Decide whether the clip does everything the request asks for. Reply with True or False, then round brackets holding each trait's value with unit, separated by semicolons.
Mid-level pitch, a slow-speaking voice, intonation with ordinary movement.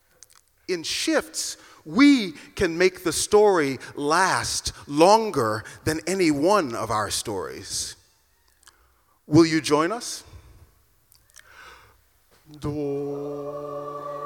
False (145 Hz; 85 wpm; 6.6 semitones)